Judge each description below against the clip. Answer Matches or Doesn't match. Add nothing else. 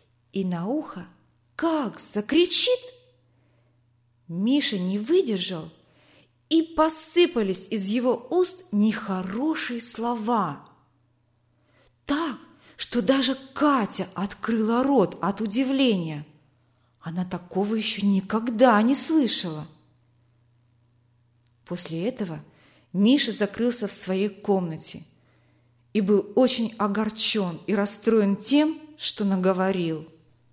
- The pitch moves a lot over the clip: Matches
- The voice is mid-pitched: Doesn't match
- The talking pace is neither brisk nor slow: Doesn't match